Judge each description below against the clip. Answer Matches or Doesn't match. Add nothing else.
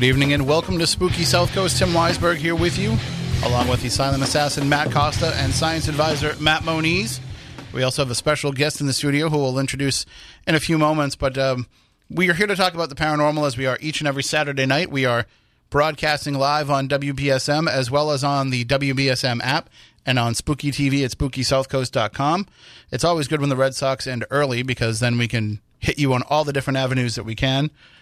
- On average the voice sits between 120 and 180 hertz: Matches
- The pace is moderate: Doesn't match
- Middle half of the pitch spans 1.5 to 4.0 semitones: Matches